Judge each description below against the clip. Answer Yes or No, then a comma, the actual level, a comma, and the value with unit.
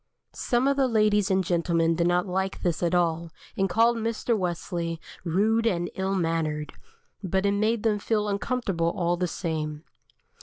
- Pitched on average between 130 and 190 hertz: Yes, medium, 185 Hz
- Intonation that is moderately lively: Yes, average, 4.0 semitones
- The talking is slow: No, average, 165 wpm